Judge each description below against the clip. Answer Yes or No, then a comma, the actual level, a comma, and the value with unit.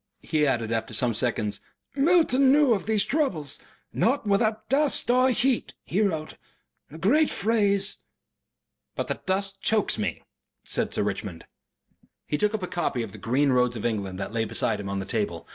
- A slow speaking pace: No, average, 180 wpm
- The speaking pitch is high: No, medium, 165 Hz